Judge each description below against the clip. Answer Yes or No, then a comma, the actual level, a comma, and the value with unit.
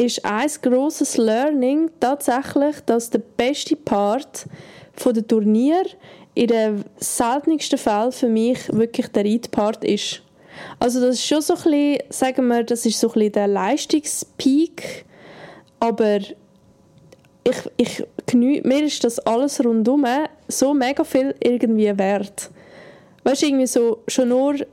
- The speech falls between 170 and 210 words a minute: No, average, 140 wpm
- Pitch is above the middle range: Yes, high, 245 Hz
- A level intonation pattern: No, average, 4.0 semitones